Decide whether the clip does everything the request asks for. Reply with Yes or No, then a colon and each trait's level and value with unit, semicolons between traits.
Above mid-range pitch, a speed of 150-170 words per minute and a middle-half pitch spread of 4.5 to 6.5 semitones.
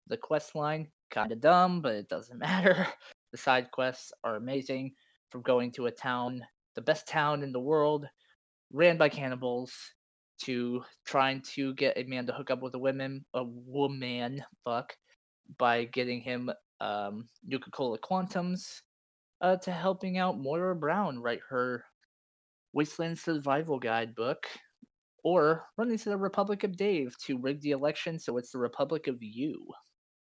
No: low, 135 Hz; average, 160 wpm; average, 5.1 semitones